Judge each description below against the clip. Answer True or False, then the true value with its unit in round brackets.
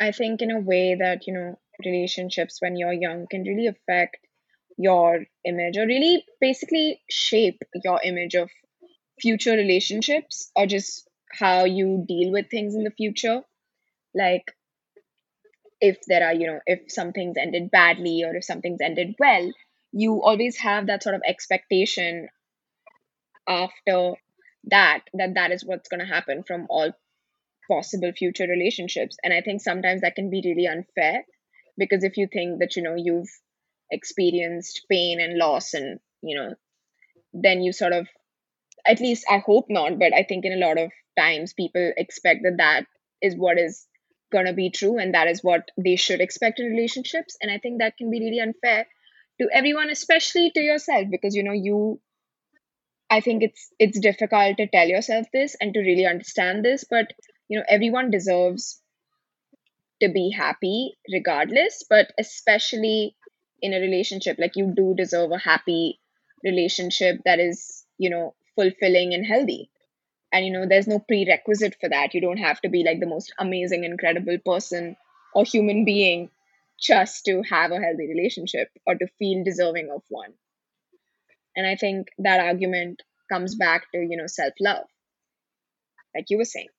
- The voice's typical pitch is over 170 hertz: True (190 Hz)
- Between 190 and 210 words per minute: False (165 wpm)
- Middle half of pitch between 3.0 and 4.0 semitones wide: True (3.6 semitones)